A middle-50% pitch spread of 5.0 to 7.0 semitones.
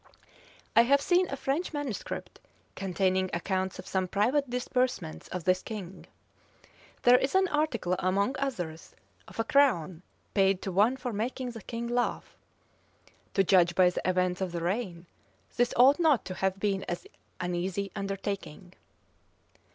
Yes: average, 5.3 semitones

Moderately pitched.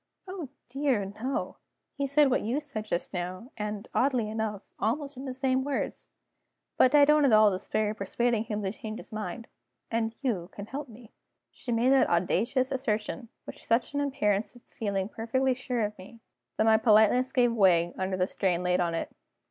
No: high, 225 Hz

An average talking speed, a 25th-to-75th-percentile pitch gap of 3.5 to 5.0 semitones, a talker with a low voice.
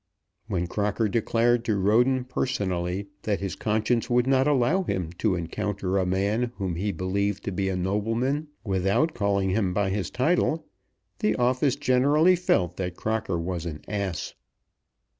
Yes: average, 155 wpm; average, 4.6 semitones; low, 105 Hz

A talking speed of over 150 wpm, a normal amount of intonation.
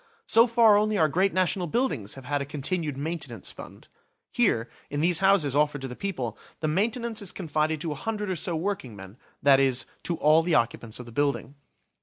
No: average, 200 wpm; wide, 6.0 semitones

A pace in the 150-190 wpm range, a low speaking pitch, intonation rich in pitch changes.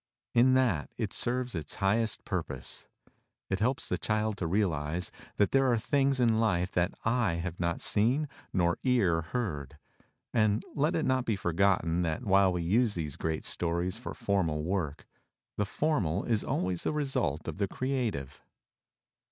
Yes: average, 160 wpm; low, 100 Hz; wide, 5.9 semitones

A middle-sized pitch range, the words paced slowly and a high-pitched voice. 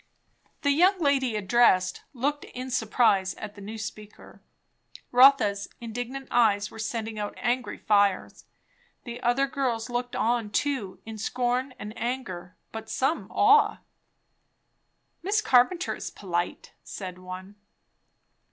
Yes: average, 3.9 semitones; slow, 125 wpm; high, 235 Hz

